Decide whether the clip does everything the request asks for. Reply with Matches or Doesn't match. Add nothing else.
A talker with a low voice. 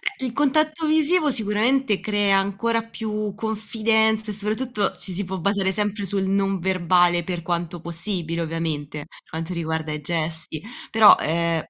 Doesn't match